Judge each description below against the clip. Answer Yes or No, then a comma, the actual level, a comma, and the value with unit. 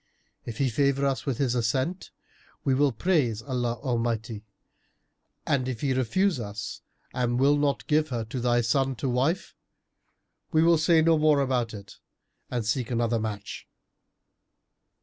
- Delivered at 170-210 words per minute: No, average, 150 wpm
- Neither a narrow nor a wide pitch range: Yes, average, 3.5 semitones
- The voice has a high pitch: No, low, 130 Hz